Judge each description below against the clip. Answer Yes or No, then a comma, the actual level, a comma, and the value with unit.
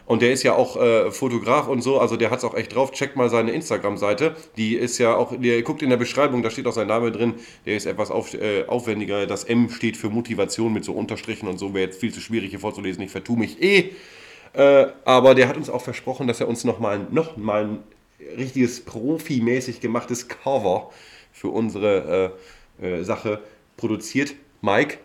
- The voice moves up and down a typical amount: Yes, average, 3.7 semitones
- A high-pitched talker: No, low, 120 Hz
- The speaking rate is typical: No, fast, 210 wpm